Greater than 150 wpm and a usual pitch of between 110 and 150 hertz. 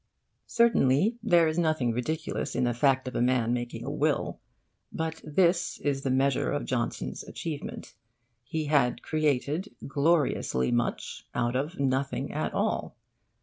No: average, 145 wpm; medium, 140 Hz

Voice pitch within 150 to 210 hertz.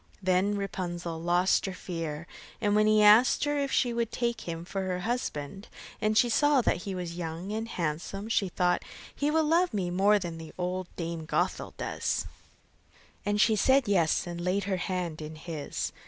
Yes: high, 190 Hz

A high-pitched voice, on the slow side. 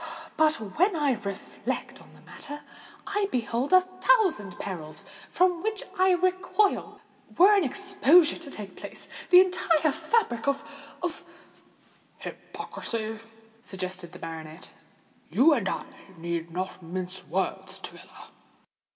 Yes: very high, 285 Hz; slow, 120 wpm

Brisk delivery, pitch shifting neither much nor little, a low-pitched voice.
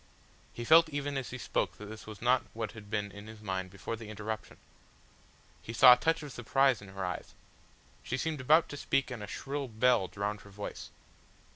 Yes: fast, 210 wpm; average, 4.6 semitones; low, 110 Hz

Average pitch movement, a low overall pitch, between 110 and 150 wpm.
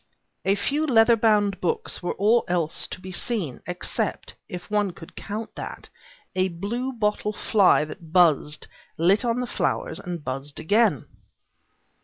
No: average, 4.5 semitones; high, 200 Hz; average, 145 wpm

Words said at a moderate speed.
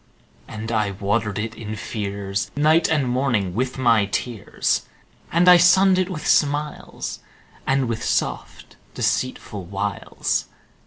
No: slow, 125 wpm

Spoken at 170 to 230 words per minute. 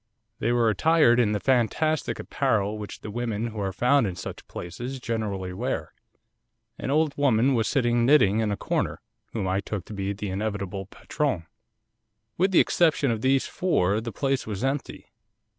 Yes: average, 175 wpm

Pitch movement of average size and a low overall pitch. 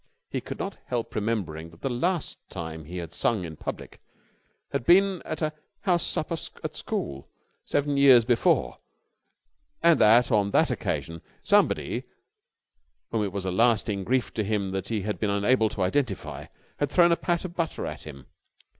No: wide, 7.2 semitones; low, 110 Hz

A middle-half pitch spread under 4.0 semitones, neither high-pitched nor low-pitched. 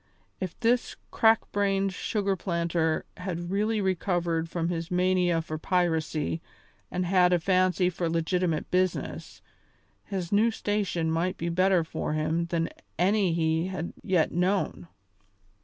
Yes: narrow, 2.4 semitones; medium, 180 Hz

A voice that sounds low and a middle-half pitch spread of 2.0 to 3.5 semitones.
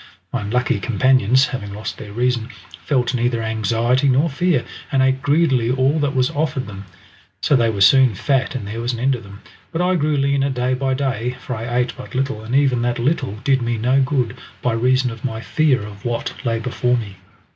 Yes: low, 125 Hz; average, 2.9 semitones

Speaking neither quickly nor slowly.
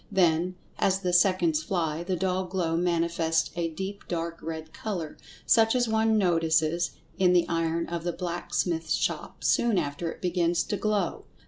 Yes: average, 160 wpm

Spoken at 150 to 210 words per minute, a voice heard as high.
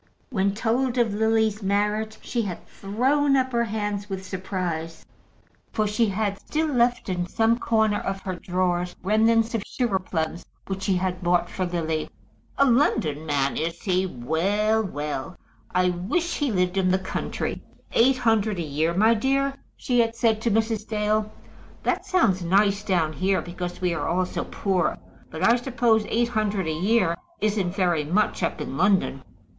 Yes: average, 170 wpm; high, 200 Hz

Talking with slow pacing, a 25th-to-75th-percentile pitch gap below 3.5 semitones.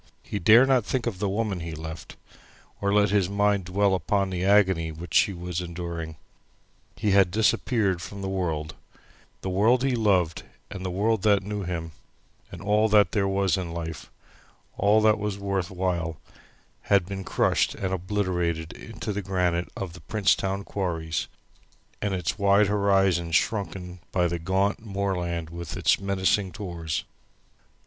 No: average, 160 wpm; average, 2.8 semitones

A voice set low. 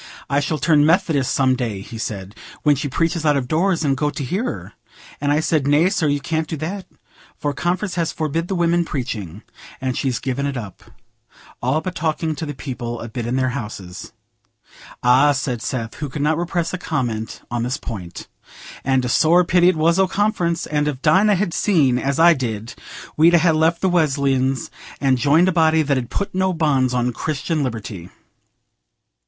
No: medium, 145 Hz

